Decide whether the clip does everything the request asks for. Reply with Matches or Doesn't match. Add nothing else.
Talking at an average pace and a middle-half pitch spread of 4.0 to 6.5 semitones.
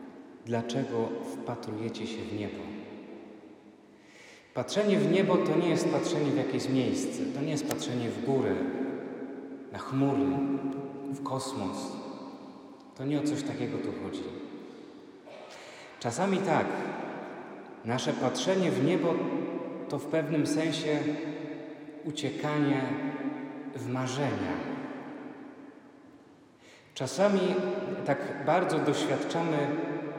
Doesn't match